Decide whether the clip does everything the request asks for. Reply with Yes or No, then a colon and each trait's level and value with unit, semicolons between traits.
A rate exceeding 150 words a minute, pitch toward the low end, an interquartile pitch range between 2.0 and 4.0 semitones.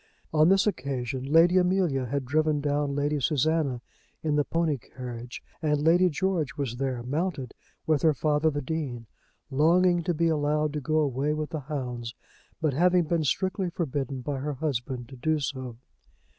No: average, 170 wpm; medium, 150 Hz; average, 3.4 semitones